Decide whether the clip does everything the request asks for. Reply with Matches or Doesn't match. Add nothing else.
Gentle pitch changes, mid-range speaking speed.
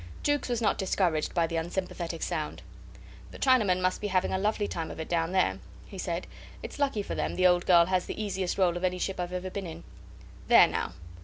Doesn't match